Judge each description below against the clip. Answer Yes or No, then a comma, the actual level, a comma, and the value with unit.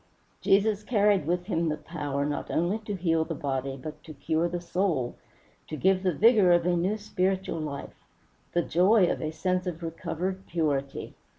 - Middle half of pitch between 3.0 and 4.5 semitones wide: Yes, average, 3.6 semitones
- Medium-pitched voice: Yes, medium, 175 Hz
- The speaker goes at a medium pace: Yes, average, 180 wpm